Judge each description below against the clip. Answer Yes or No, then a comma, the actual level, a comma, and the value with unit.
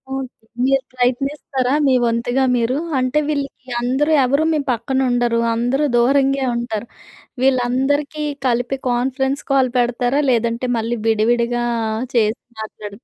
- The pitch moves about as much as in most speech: No, narrow, 2.2 semitones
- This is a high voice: Yes, very high, 250 Hz